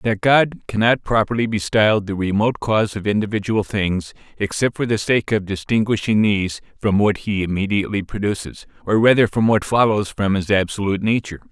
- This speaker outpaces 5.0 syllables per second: Yes, 5.6 syllables/s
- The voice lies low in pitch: Yes, low, 105 Hz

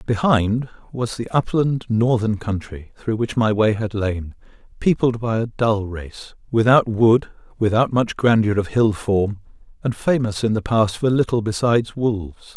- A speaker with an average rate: Yes, average, 160 wpm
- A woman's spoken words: No, male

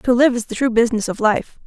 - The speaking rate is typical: No, fast, 290 wpm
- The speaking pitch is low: No, high, 235 Hz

